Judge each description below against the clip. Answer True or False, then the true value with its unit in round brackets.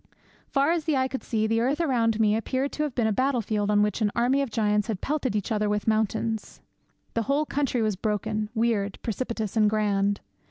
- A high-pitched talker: True (225 Hz)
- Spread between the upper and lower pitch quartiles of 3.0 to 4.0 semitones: True (3.7 semitones)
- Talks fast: True (215 wpm)